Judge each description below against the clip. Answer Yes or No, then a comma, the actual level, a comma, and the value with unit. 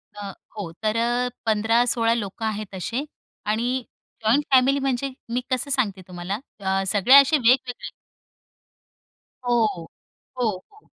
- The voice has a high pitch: Yes, high, 230 Hz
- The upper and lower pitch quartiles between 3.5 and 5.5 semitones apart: Yes, average, 3.8 semitones